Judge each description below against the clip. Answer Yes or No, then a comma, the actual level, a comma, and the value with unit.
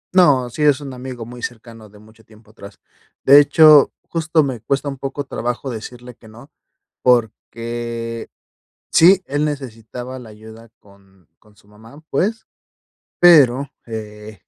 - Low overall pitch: Yes, low, 120 Hz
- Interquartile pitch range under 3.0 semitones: No, average, 4.2 semitones